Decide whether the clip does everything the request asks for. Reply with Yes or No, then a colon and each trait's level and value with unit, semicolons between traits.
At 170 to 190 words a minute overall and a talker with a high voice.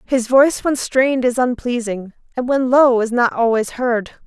Yes: average, 185 wpm; high, 245 Hz